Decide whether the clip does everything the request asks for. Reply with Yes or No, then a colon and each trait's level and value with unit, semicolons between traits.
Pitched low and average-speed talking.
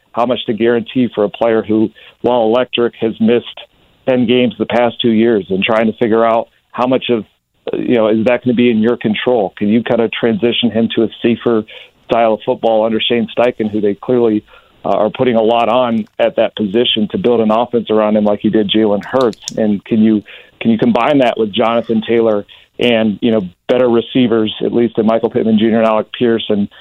No: low, 115 Hz; fast, 220 wpm